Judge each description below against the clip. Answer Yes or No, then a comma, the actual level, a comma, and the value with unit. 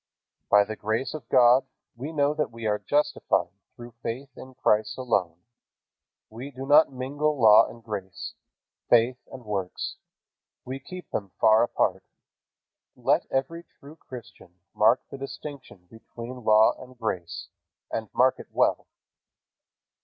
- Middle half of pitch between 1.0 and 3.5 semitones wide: No, average, 3.9 semitones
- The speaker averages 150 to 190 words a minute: No, average, 140 wpm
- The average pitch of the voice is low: Yes, low, 120 Hz